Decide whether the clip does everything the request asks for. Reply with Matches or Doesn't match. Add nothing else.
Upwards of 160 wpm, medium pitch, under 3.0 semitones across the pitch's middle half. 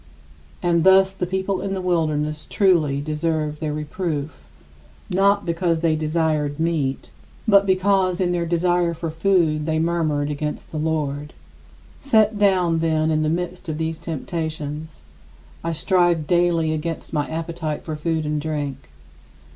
Doesn't match